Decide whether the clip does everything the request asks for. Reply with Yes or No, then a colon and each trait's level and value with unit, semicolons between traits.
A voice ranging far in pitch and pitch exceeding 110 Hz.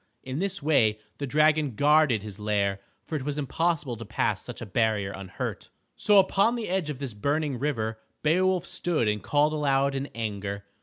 Yes: wide, 6.2 semitones; medium, 140 Hz